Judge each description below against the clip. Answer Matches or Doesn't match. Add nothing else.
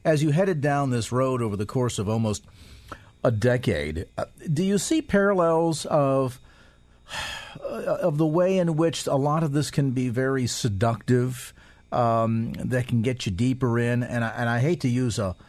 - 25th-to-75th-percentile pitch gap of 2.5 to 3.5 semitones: Doesn't match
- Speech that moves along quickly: Doesn't match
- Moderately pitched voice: Doesn't match